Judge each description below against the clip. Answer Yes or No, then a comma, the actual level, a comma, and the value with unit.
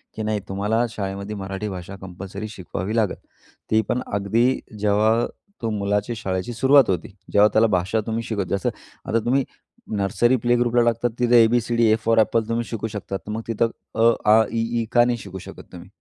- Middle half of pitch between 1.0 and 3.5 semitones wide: Yes, average, 2.8 semitones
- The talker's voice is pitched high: No, low, 110 Hz